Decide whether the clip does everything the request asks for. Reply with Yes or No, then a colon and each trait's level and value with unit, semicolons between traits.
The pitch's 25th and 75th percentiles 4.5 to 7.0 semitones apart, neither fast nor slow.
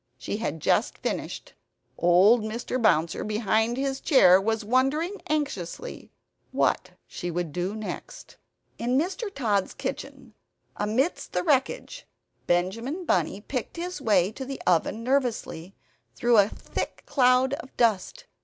No: wide, 5.4 semitones; slow, 130 wpm